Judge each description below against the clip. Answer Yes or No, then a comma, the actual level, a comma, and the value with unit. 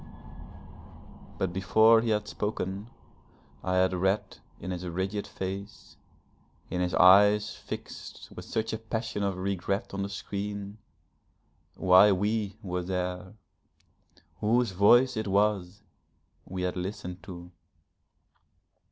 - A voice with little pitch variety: Yes, narrow, 2.3 semitones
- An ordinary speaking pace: No, slow, 115 wpm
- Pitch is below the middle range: Yes, low, 100 Hz